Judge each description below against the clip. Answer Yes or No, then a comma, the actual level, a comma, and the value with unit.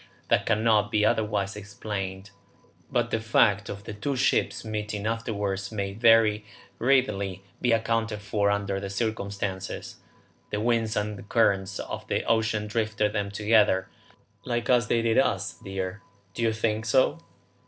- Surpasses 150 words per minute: No, average, 145 wpm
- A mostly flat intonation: Yes, narrow, 2.1 semitones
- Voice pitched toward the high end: No, low, 105 Hz